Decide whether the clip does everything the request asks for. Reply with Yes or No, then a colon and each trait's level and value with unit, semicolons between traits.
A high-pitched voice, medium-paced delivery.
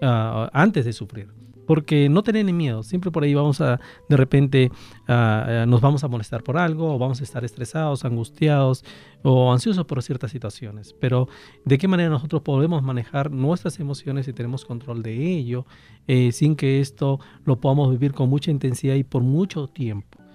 No: low, 135 Hz; average, 185 wpm